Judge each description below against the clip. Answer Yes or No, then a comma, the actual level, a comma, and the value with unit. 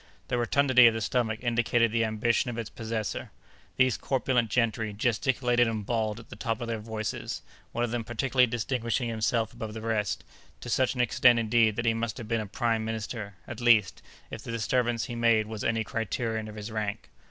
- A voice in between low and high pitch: No, low, 115 Hz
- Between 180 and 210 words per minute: Yes, average, 190 wpm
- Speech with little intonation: Yes, narrow, 1.5 semitones